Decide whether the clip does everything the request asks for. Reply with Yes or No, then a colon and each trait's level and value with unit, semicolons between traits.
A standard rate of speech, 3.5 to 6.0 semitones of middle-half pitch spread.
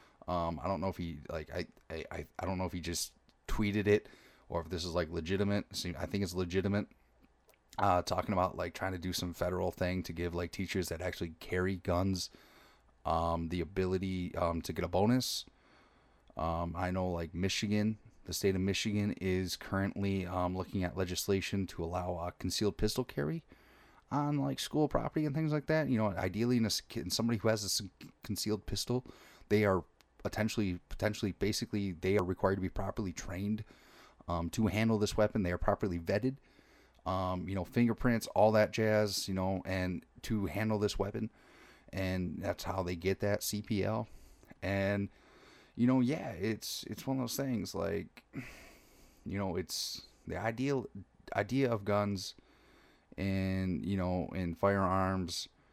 No: average, 175 wpm; average, 3.0 semitones